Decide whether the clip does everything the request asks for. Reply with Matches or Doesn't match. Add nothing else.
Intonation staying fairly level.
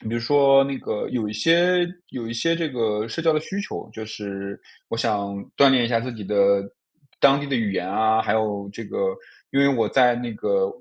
Doesn't match